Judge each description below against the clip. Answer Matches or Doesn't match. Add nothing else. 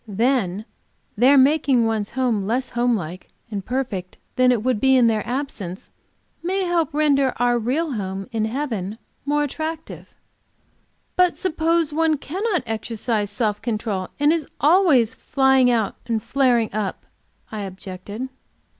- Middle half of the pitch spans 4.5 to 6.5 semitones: Matches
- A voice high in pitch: Matches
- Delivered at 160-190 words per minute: Doesn't match